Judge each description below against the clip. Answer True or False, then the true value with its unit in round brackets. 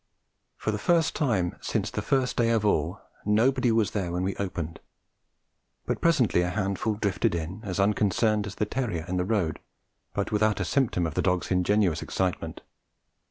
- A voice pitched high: False (100 Hz)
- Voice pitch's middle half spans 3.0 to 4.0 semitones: True (3.5 semitones)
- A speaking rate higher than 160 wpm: True (175 wpm)